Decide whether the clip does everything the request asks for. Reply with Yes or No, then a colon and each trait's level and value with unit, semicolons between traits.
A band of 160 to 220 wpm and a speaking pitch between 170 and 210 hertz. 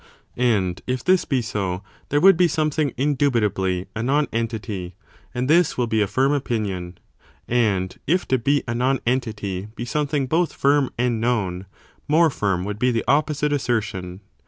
No: average, 165 wpm; low, 120 Hz